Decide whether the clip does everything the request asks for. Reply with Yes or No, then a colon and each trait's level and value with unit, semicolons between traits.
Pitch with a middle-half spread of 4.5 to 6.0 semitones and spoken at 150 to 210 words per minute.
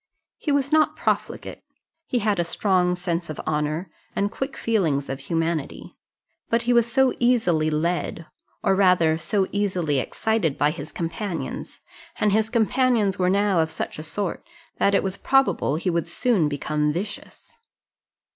Yes: wide, 5.4 semitones; average, 155 wpm